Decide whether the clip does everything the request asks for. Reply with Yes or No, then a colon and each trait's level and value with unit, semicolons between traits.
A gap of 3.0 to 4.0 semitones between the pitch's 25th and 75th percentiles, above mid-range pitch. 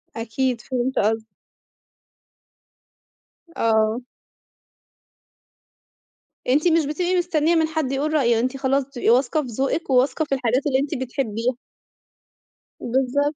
Yes: average, 3.6 semitones; very high, 265 Hz